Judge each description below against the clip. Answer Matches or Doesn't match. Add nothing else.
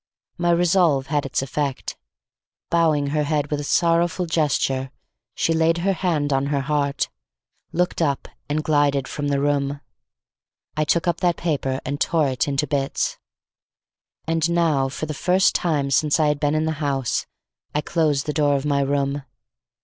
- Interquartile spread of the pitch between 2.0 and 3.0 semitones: Matches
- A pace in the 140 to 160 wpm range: Doesn't match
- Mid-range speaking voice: Matches